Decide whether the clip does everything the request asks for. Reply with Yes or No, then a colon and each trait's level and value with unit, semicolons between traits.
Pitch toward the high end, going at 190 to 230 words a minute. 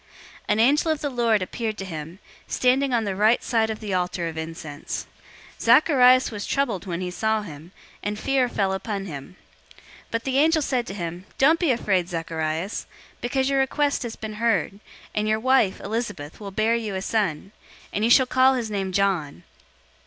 Yes: high, 215 Hz; average, 195 wpm